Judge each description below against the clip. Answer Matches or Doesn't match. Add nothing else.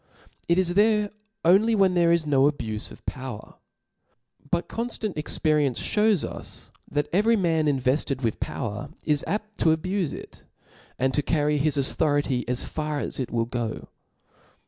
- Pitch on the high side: Doesn't match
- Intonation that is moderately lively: Doesn't match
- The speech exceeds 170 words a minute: Doesn't match